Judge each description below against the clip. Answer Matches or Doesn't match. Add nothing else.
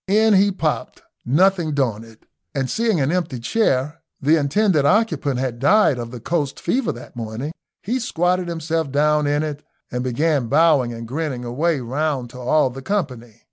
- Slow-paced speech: Doesn't match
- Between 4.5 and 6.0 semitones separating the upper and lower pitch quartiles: Matches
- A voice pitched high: Doesn't match